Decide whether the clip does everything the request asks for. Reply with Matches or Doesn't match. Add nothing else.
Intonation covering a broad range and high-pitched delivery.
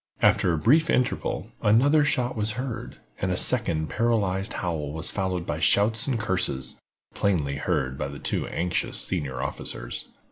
Doesn't match